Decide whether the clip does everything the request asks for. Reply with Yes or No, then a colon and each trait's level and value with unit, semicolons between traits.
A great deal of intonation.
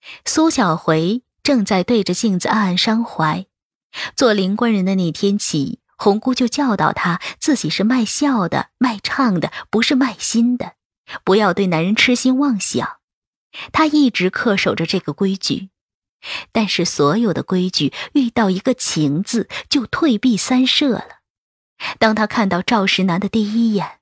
No: average, 5.0 semitones